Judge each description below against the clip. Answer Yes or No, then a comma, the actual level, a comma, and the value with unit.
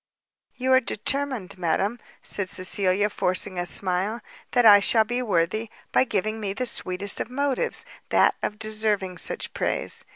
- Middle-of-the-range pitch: No, high, 210 Hz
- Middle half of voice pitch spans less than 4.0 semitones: No, average, 4.4 semitones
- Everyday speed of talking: Yes, average, 155 wpm